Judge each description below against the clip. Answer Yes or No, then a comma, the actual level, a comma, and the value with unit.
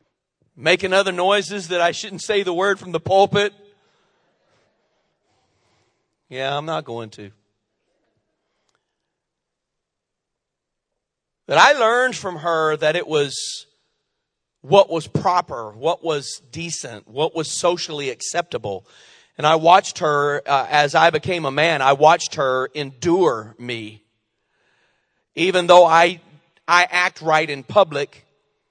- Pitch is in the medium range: Yes, medium, 160 Hz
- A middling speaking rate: No, slow, 120 wpm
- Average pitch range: Yes, average, 4.3 semitones